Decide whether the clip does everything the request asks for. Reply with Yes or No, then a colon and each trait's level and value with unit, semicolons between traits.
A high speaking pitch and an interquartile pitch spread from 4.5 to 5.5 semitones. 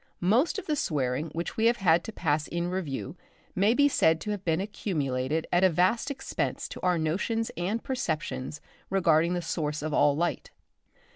No: medium, 175 Hz; average, 4.9 semitones